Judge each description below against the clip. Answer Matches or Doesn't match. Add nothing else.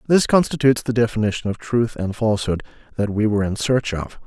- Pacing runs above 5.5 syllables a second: Matches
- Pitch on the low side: Matches